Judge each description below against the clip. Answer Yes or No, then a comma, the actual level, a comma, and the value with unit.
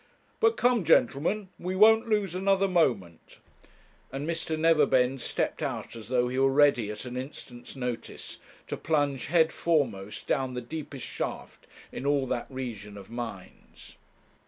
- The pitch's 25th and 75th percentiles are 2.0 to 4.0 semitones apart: No, average, 5.3 semitones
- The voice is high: No, low, 135 Hz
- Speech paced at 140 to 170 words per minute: Yes, average, 150 wpm